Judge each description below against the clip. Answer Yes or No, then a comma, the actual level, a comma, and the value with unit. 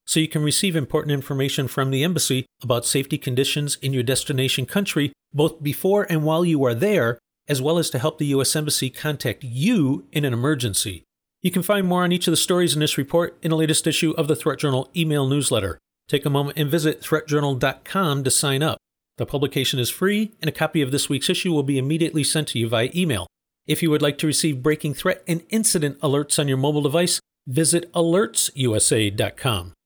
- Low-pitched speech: No, medium, 150 Hz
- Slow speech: No, fast, 205 wpm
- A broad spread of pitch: No, average, 3.2 semitones